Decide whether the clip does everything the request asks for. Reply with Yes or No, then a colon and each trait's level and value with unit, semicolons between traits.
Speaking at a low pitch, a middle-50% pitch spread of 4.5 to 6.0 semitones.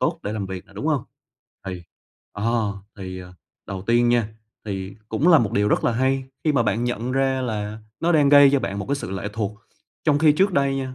Yes: low, 115 Hz; average, 5.1 semitones